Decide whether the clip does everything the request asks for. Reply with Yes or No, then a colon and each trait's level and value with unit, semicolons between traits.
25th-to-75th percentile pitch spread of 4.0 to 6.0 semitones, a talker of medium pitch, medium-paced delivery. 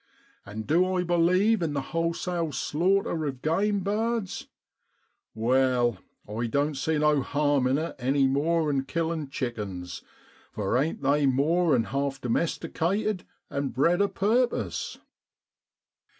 No: average, 4.7 semitones; medium, 150 Hz; slow, 130 wpm